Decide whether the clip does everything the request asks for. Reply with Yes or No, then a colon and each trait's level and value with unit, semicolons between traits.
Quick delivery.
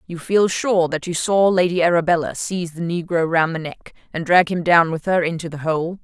Yes: fast, 230 wpm